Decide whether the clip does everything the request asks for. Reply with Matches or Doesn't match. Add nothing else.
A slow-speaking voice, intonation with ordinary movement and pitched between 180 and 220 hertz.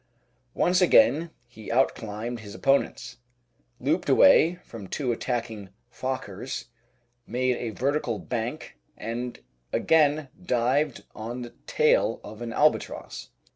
Doesn't match